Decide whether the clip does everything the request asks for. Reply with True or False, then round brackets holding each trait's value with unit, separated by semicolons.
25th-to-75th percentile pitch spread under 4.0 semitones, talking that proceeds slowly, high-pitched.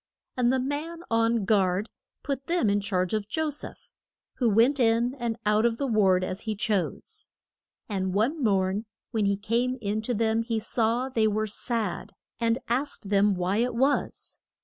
False (3.2 semitones; 175 wpm; 225 Hz)